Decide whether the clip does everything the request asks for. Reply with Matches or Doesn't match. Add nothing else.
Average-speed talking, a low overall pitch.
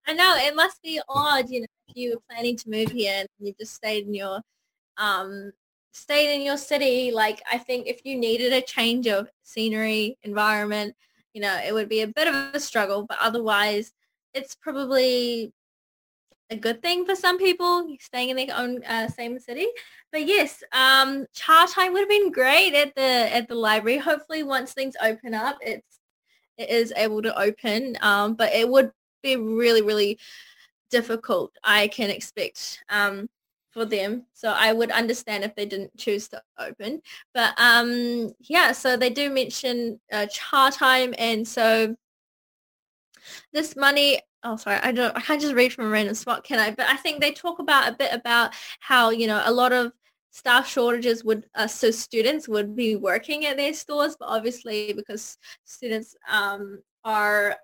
Doesn't match